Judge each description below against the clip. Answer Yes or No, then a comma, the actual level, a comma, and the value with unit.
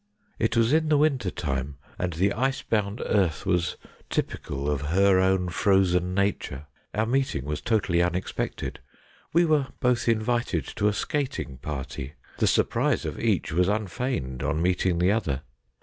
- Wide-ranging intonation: Yes, wide, 5.9 semitones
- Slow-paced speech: No, average, 155 wpm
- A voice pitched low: Yes, very low, 95 Hz